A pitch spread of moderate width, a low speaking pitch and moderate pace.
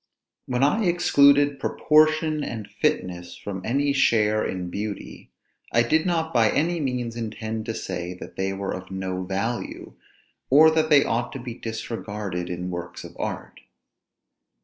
No: wide, 6.8 semitones; low, 115 Hz; average, 150 wpm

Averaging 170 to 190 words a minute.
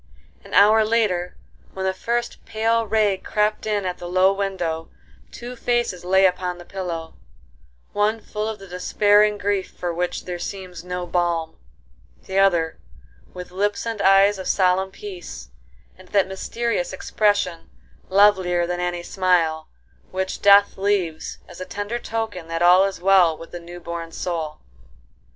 No: average, 155 wpm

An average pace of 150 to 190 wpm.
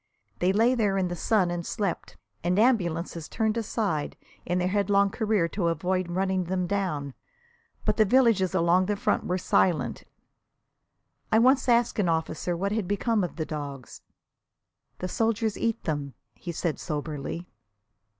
Yes: average, 155 wpm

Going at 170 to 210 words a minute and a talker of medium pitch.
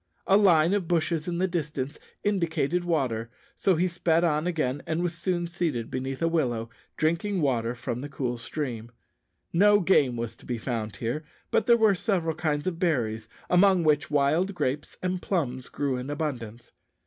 Yes: average, 175 wpm; medium, 155 Hz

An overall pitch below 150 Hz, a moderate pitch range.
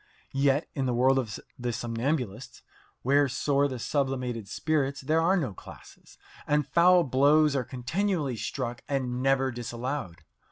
Yes: low, 135 Hz; average, 3.0 semitones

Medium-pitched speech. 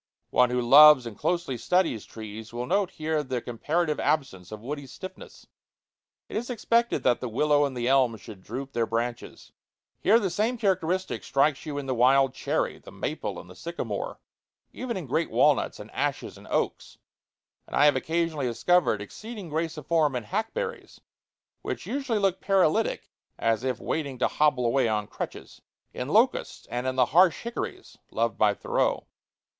Yes: medium, 145 Hz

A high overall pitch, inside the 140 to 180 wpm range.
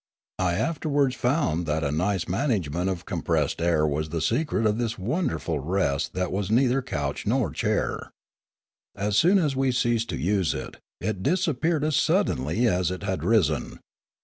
No: low, 100 Hz; average, 165 wpm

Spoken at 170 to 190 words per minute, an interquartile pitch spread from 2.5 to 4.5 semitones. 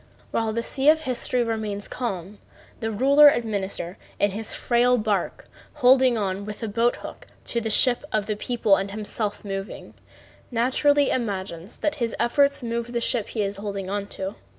Yes: average, 175 wpm; average, 3.4 semitones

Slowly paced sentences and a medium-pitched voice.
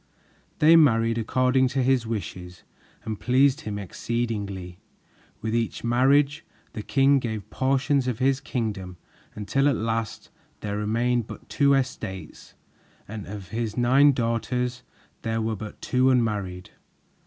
No: slow, 130 wpm; low, 115 Hz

